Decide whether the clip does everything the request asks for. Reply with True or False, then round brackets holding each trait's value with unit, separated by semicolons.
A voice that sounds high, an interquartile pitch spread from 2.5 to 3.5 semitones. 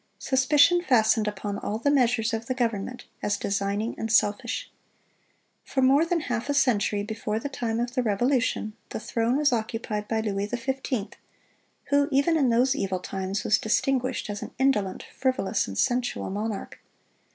False (230 Hz; 4.0 semitones)